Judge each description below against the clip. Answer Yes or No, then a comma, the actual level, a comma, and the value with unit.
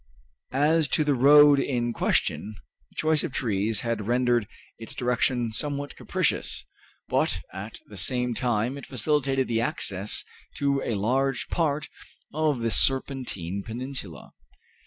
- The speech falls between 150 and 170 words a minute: No, slow, 135 wpm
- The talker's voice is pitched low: Yes, low, 125 Hz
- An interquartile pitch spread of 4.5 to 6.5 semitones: No, average, 3.8 semitones